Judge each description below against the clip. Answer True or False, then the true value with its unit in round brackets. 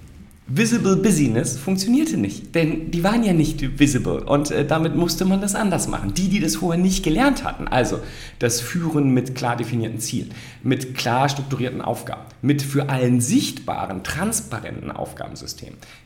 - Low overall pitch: False (145 Hz)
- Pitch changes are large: True (6.3 semitones)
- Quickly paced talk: False (155 wpm)